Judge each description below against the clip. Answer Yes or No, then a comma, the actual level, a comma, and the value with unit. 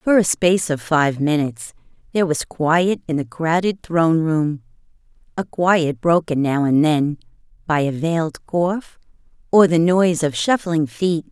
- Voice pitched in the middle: Yes, medium, 160 Hz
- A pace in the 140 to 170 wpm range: Yes, average, 160 wpm